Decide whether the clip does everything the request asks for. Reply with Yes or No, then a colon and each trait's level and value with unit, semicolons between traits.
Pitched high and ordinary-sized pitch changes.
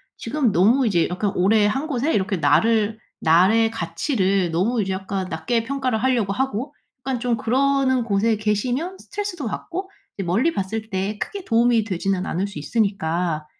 Yes: high, 220 Hz; average, 5.0 semitones